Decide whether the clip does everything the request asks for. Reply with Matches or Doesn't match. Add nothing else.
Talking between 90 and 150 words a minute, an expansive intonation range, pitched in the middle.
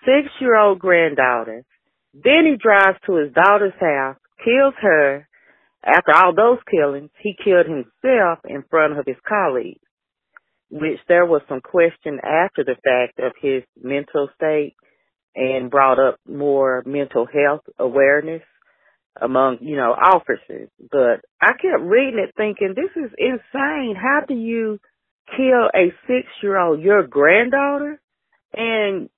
Matches